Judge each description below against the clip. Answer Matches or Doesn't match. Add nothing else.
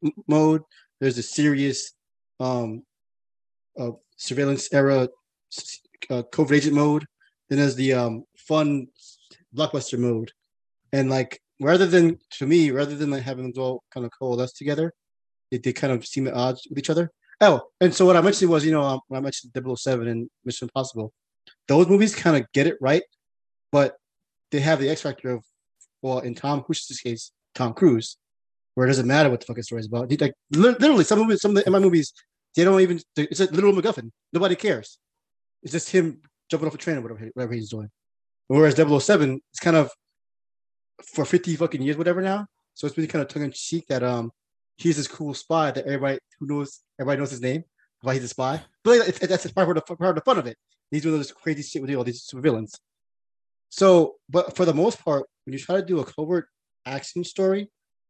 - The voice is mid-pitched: Matches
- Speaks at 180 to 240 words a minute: Matches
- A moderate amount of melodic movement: Matches